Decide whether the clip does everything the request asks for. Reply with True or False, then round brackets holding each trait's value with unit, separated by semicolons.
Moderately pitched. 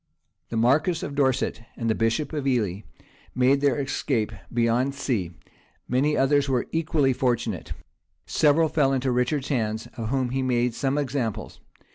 False (130 Hz)